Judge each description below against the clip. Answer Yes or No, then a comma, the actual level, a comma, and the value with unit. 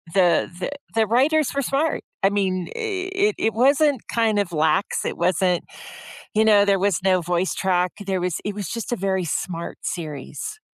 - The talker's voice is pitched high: Yes, high, 200 Hz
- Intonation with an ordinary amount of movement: No, wide, 5.8 semitones